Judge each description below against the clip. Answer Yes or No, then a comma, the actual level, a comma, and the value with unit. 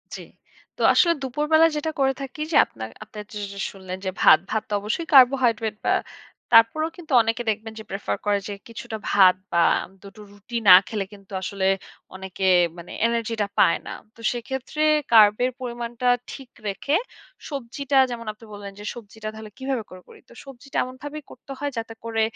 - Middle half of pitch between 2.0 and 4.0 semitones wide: No, average, 4.4 semitones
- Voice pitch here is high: Yes, high, 230 Hz